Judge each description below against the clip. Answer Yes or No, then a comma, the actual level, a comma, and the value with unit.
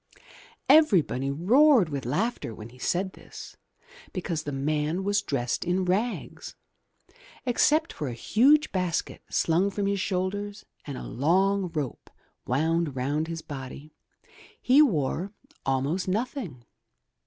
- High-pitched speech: No, medium, 175 Hz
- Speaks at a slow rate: Yes, slow, 125 wpm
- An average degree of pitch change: No, wide, 6.0 semitones